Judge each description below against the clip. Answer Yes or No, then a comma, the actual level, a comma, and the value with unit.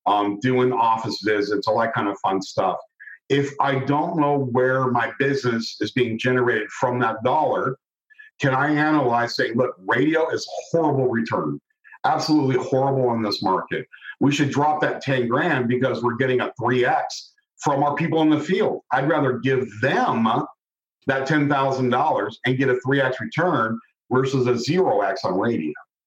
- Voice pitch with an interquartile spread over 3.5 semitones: No, average, 3.1 semitones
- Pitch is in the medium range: No, low, 130 Hz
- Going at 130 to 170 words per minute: Yes, average, 165 wpm